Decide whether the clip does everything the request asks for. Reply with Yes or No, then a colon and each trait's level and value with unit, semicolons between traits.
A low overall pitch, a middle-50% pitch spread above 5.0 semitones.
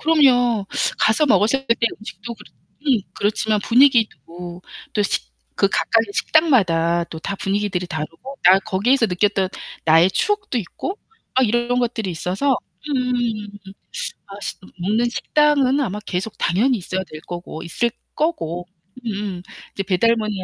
No: high, 215 Hz; wide, 5.4 semitones